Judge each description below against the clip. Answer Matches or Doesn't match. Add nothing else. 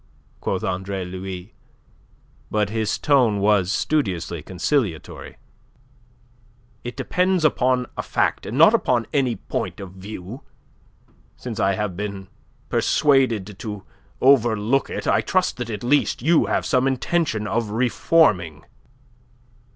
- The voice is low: Matches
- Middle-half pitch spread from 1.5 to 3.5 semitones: Doesn't match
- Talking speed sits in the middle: Doesn't match